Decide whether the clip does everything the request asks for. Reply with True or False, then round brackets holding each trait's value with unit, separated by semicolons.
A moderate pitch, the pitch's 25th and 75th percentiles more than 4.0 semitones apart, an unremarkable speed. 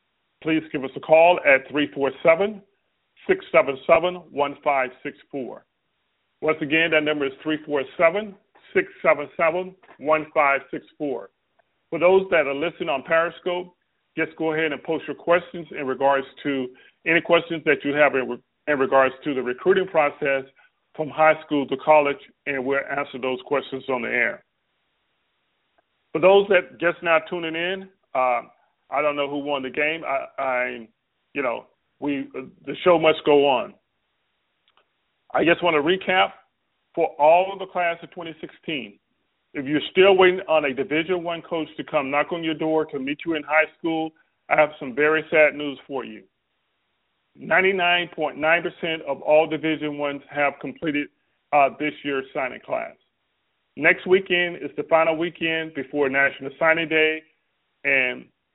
False (155 Hz; 3.3 semitones; 160 wpm)